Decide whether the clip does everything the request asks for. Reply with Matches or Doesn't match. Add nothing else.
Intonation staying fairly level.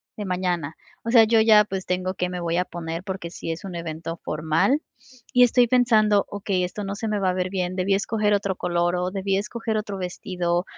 Doesn't match